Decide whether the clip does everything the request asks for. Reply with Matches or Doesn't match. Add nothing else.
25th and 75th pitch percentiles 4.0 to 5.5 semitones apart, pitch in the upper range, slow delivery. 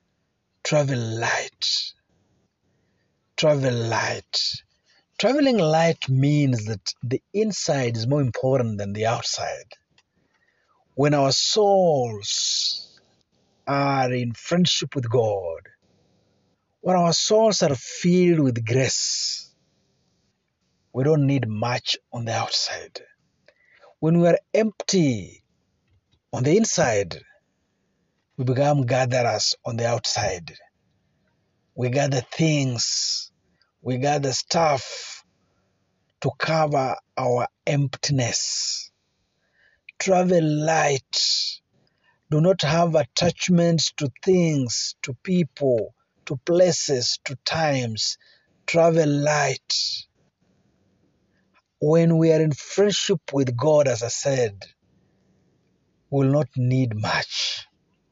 Doesn't match